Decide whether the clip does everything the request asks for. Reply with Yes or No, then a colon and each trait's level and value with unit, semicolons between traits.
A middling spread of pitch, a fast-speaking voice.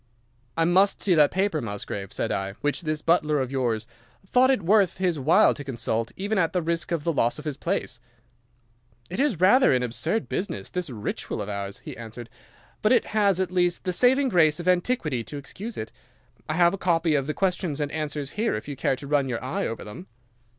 No: wide, 6.1 semitones; fast, 215 wpm